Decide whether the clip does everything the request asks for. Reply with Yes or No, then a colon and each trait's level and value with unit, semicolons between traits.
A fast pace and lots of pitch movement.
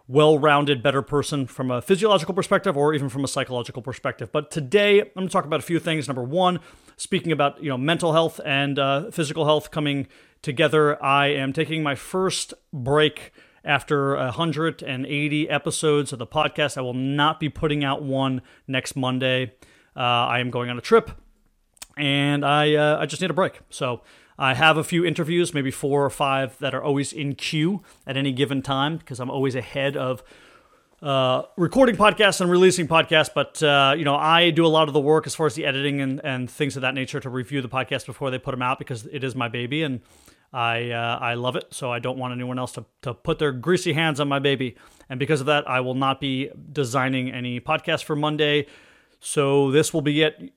No: fast, 210 wpm; average, 3.0 semitones